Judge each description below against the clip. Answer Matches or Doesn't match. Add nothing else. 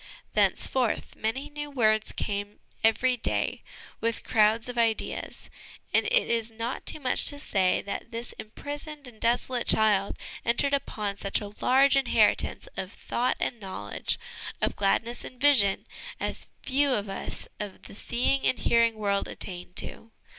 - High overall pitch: Matches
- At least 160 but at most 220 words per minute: Doesn't match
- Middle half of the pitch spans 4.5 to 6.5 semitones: Doesn't match